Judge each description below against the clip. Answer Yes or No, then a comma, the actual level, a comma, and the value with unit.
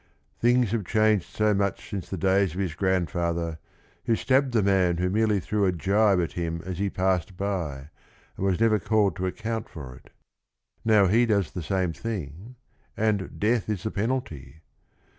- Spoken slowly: No, average, 180 wpm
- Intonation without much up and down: No, average, 3.7 semitones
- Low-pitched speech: Yes, very low, 95 Hz